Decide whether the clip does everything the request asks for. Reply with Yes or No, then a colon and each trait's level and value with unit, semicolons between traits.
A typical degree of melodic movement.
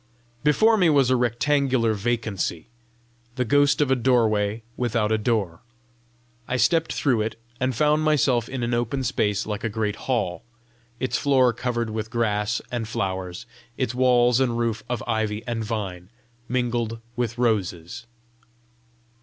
Yes: average, 3.0 semitones